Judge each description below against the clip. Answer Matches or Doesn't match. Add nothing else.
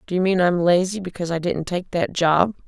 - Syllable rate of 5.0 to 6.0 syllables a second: Matches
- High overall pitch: Doesn't match